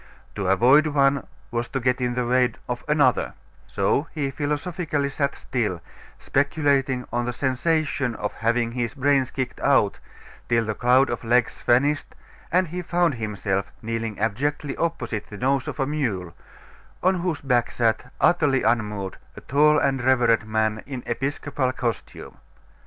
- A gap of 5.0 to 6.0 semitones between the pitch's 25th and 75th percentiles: No, average, 3.7 semitones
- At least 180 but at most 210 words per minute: No, average, 150 wpm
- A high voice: No, low, 130 Hz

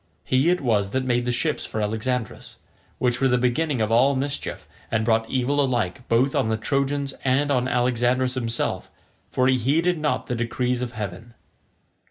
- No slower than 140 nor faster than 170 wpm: No, average, 180 wpm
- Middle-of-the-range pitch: No, low, 125 Hz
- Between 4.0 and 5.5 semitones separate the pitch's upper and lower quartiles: No, narrow, 2.5 semitones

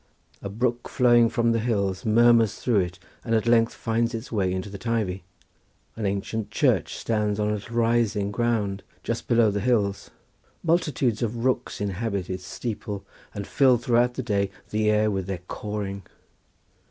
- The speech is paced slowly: No, average, 165 wpm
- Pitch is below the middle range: Yes, low, 110 Hz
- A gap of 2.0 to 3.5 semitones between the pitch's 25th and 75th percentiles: Yes, average, 2.9 semitones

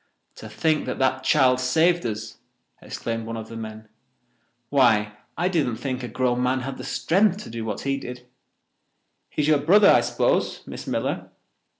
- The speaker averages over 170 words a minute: Yes, average, 180 wpm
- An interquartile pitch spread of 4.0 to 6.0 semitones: Yes, average, 4.6 semitones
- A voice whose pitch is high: No, low, 130 Hz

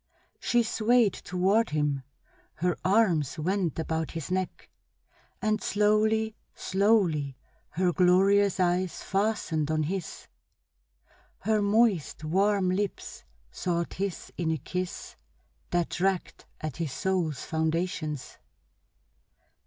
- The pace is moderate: No, slow, 105 wpm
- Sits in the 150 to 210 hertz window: Yes, medium, 185 Hz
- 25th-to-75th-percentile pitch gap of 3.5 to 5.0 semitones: Yes, average, 4.0 semitones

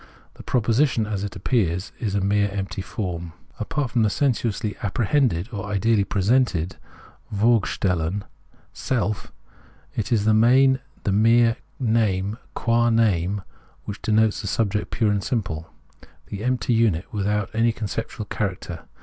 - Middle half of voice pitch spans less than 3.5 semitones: Yes, average, 2.9 semitones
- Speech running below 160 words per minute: Yes, average, 140 wpm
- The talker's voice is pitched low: Yes, low, 105 Hz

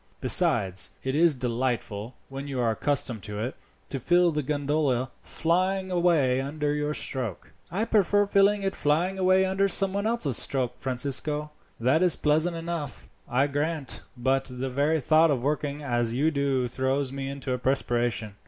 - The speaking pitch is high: No, medium, 145 Hz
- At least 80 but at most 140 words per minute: No, average, 165 wpm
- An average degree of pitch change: Yes, average, 4.5 semitones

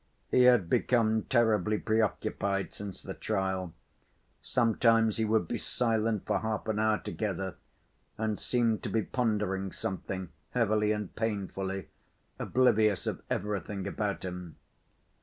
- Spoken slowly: Yes, slow, 125 wpm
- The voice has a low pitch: Yes, low, 105 Hz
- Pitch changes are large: No, narrow, 2.5 semitones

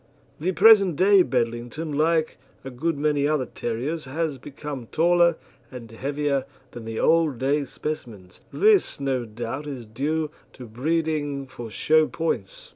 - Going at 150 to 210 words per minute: No, average, 140 wpm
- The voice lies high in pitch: No, medium, 145 Hz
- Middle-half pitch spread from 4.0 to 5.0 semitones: Yes, average, 4.5 semitones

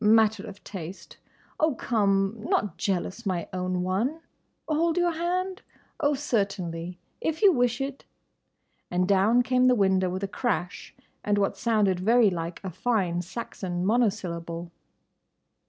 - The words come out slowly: Yes, slow, 125 wpm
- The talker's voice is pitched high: Yes, high, 205 Hz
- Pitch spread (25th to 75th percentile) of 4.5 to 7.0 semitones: Yes, average, 5.1 semitones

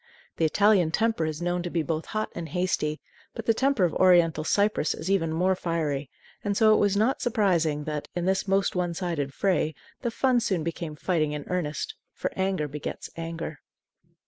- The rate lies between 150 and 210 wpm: Yes, average, 190 wpm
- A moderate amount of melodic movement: Yes, average, 4.0 semitones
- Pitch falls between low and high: Yes, medium, 175 Hz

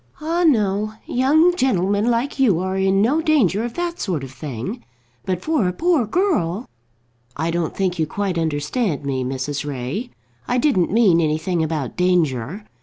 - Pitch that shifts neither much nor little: No, wide, 7.8 semitones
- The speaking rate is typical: Yes, average, 170 wpm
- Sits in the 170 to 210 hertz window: Yes, high, 190 Hz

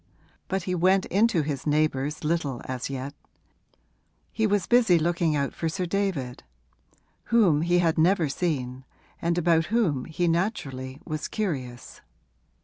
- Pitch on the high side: No, medium, 165 Hz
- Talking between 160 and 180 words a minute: No, average, 140 wpm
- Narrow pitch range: No, average, 4.6 semitones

